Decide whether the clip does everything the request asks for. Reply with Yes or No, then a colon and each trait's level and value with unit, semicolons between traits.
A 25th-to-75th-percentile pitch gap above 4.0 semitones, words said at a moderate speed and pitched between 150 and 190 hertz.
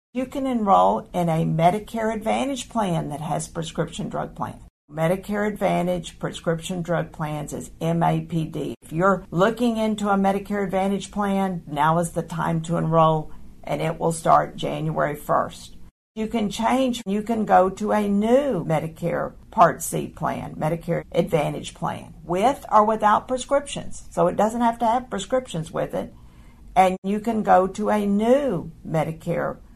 Yes: average, 4.4 semitones; average, 155 wpm; medium, 185 Hz